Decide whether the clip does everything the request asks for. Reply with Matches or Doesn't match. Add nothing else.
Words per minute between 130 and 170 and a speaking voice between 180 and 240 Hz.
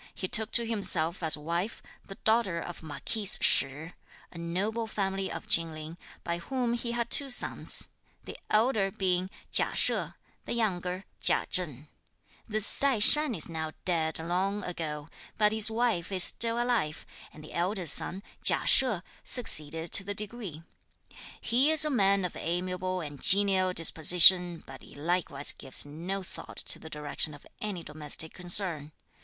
Matches